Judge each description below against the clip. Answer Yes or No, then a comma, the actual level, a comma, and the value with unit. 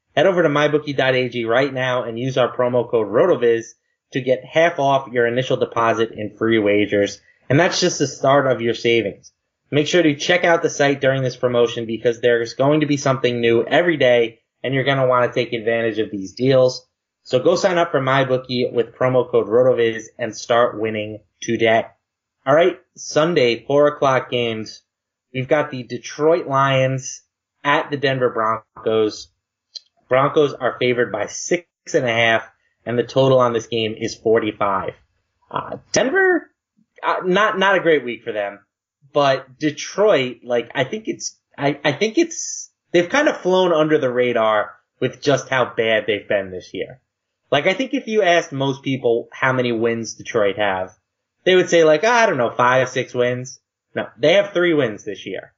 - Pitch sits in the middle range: No, low, 130 Hz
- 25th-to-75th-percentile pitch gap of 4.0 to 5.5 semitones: Yes, average, 4.6 semitones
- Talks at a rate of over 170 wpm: Yes, average, 185 wpm